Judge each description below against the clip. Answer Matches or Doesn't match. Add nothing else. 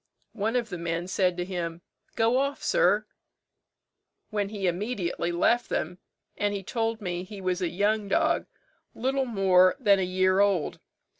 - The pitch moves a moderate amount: Matches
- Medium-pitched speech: Doesn't match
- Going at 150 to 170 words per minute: Matches